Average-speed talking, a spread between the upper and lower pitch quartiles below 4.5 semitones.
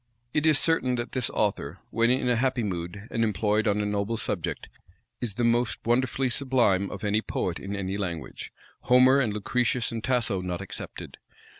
Yes: average, 180 wpm; average, 3.8 semitones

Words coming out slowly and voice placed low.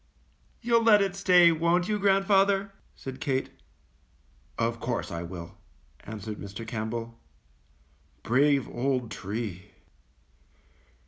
Yes: slow, 105 wpm; low, 130 Hz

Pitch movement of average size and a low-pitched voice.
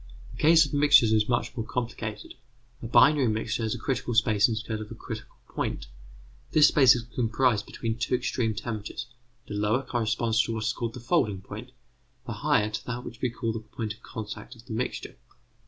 No: narrow, 2.2 semitones; low, 115 Hz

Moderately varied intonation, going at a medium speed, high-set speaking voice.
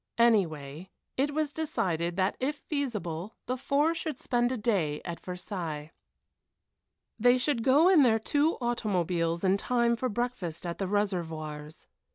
No: wide, 7.0 semitones; average, 145 wpm; high, 210 Hz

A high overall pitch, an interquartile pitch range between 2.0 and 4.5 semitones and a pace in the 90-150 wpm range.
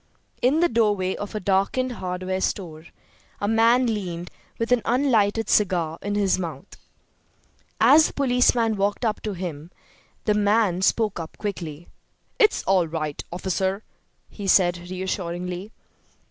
Yes: high, 195 Hz; average, 4.0 semitones; slow, 135 wpm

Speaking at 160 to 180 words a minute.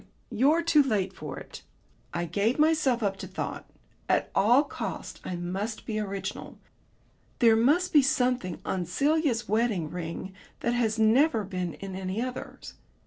No: average, 150 wpm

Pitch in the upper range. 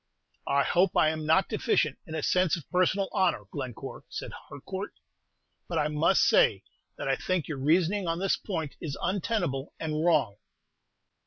No: medium, 165 Hz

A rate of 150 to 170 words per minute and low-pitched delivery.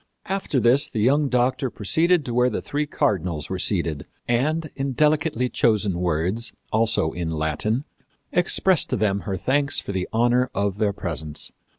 Yes: average, 165 wpm; low, 115 Hz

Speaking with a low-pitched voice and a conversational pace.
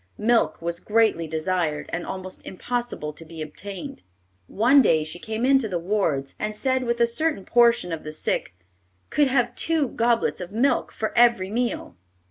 No: high, 210 Hz; average, 170 wpm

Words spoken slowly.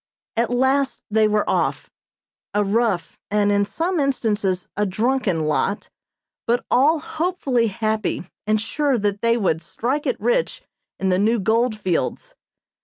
No: average, 145 wpm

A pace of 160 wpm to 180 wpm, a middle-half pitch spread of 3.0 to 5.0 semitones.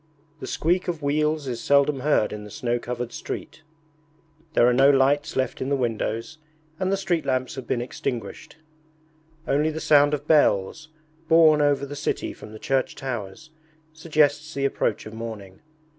Yes: average, 170 wpm; average, 4.0 semitones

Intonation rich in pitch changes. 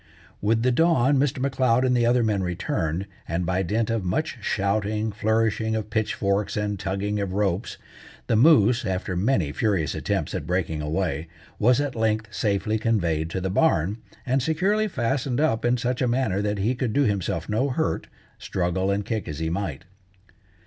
No: average, 4.5 semitones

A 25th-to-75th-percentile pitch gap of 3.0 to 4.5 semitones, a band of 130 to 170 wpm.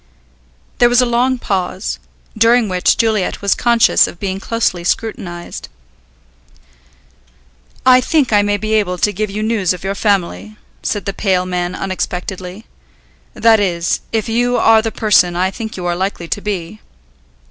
Yes: average, 3.6 semitones; average, 160 wpm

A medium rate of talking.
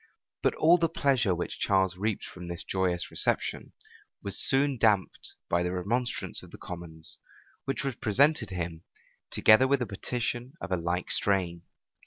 Yes: average, 160 wpm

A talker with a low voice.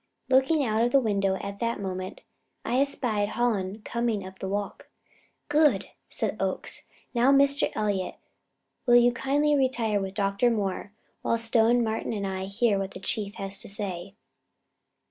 No: high, 215 Hz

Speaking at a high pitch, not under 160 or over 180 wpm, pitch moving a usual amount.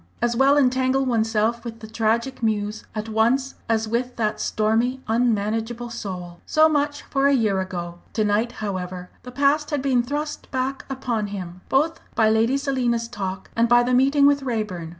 Yes: high, 235 Hz; average, 175 wpm; average, 3.7 semitones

